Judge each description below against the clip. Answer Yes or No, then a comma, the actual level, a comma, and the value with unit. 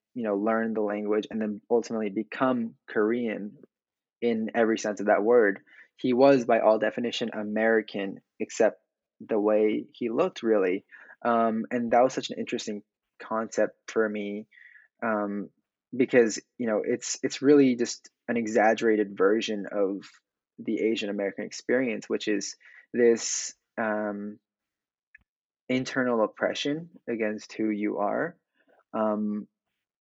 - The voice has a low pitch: Yes, low, 110 Hz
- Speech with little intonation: Yes, narrow, 1.9 semitones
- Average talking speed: No, slow, 130 wpm